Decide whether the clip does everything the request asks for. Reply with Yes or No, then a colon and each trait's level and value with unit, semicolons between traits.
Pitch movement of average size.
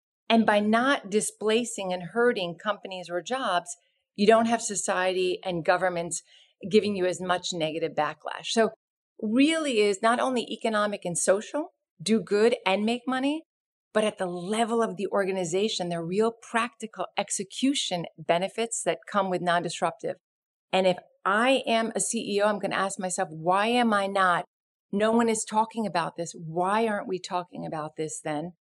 Yes: average, 4.0 semitones